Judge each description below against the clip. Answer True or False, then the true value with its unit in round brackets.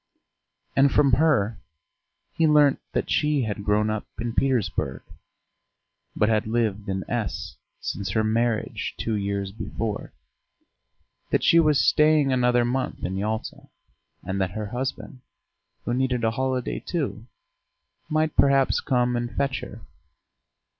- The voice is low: True (120 Hz)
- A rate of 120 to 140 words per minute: True (135 wpm)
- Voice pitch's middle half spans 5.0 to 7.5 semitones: False (4.3 semitones)